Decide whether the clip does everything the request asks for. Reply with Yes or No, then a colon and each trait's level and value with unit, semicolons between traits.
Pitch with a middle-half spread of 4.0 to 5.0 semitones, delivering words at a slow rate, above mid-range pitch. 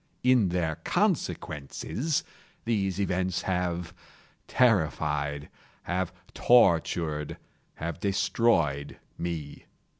No: average, 4.3 semitones; slow, 60 wpm; very low, 90 Hz